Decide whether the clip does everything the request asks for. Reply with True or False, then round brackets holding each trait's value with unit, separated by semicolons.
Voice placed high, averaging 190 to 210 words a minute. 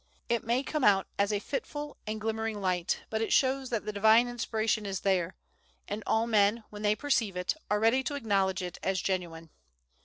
True (215 Hz; 195 wpm)